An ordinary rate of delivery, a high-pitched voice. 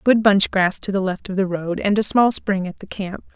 No: fast, 285 wpm; high, 195 Hz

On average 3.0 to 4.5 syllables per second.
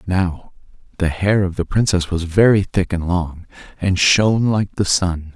Yes: 4.3 syllables/s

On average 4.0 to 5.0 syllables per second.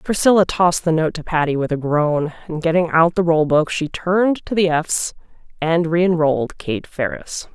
Yes: 4.9 syllables/s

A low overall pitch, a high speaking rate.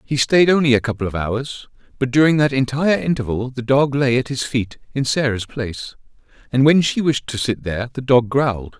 Yes: low, 130 Hz; fast, 210 wpm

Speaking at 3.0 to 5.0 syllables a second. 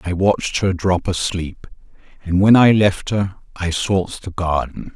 Yes: 4.1 syllables/s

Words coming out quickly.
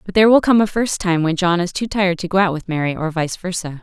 Yes: fast, 315 wpm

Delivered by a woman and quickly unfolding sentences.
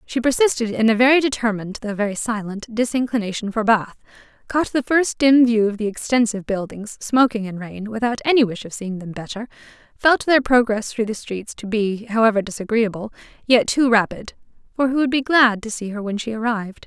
No: female; average, 195 wpm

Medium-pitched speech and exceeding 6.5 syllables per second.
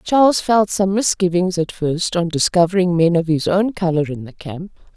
No: medium, 180 Hz; 5.0 syllables/s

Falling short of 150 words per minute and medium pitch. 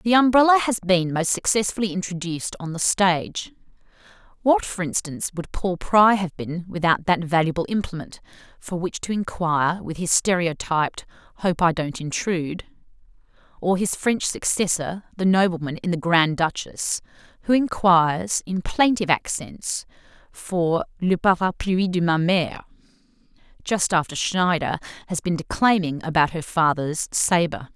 Yes: average, 140 wpm; medium, 180 Hz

